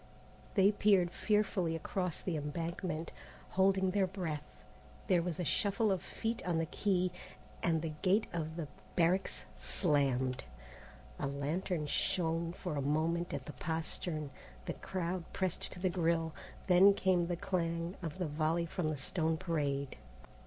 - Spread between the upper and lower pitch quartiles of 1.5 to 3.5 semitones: Yes, average, 2.9 semitones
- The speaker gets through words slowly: No, average, 150 wpm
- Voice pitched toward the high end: No, medium, 170 Hz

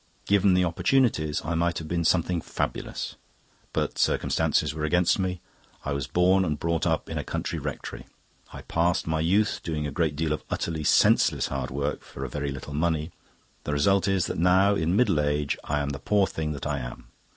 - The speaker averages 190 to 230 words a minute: Yes, average, 200 wpm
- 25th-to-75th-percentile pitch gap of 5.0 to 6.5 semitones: No, average, 3.6 semitones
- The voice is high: No, very low, 80 Hz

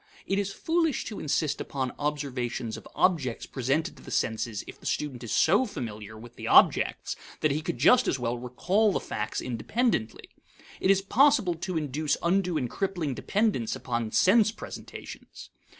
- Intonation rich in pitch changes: Yes, wide, 8.1 semitones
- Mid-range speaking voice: Yes, medium, 150 Hz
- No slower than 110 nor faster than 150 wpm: No, average, 165 wpm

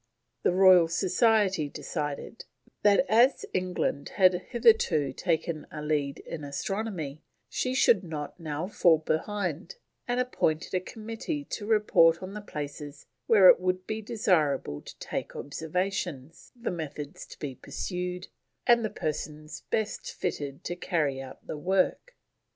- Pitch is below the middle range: No, medium, 180 Hz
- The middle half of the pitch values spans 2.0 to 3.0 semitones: No, wide, 5.5 semitones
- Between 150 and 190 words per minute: No, average, 140 wpm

